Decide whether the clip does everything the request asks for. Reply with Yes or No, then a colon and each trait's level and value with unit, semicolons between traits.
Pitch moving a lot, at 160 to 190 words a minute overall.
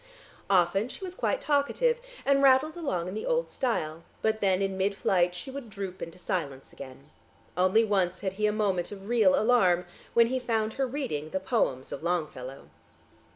Yes: wide, 5.9 semitones; average, 180 wpm